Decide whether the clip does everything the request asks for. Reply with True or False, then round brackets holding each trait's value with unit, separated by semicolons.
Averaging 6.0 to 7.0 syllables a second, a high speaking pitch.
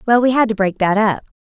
True (6.3 syllables/s; 215 Hz)